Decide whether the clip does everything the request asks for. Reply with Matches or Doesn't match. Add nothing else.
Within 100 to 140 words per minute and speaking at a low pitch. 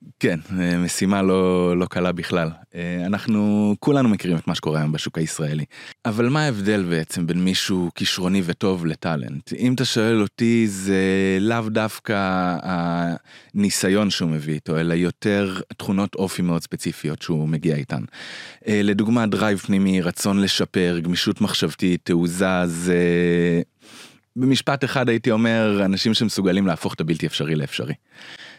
Matches